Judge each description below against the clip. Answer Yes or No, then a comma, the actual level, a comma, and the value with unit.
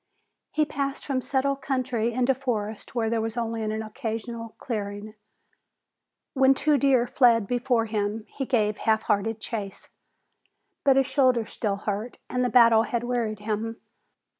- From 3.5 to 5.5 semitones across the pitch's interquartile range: No, average, 2.9 semitones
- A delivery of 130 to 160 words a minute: Yes, average, 145 wpm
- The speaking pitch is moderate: No, high, 230 Hz